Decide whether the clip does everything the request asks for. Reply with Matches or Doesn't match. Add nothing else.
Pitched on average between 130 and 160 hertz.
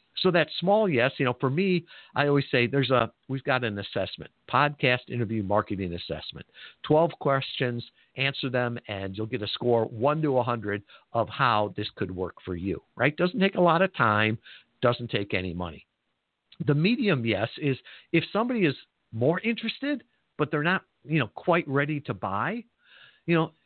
Matches